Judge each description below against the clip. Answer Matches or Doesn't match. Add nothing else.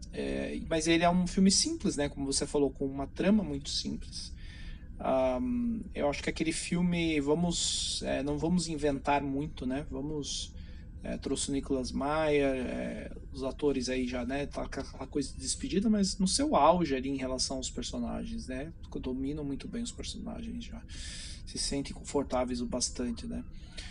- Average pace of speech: Matches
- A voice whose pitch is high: Doesn't match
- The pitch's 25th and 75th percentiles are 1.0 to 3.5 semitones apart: Doesn't match